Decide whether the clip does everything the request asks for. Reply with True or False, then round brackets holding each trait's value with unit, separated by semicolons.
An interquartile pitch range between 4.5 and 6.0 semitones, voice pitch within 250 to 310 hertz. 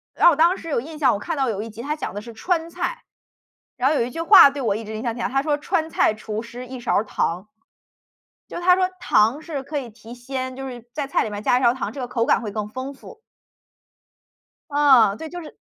True (5.0 semitones; 260 Hz)